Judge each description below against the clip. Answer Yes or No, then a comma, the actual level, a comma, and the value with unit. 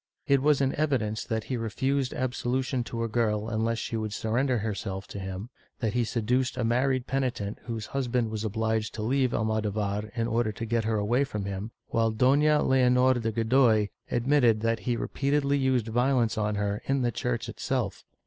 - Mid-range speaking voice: No, low, 115 Hz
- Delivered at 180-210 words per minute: Yes, average, 185 wpm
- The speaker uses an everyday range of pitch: Yes, average, 3.0 semitones